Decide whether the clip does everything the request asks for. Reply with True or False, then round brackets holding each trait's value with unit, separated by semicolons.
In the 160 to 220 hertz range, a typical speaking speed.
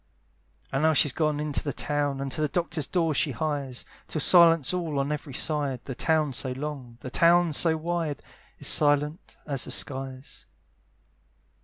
False (150 Hz; 170 wpm)